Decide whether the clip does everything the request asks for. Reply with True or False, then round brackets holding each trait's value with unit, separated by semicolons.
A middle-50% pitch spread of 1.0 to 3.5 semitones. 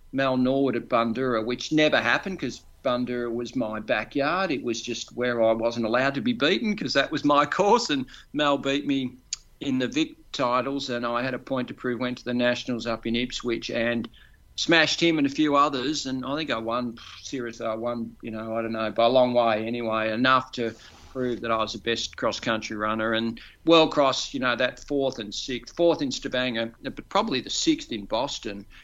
True (3.1 semitones)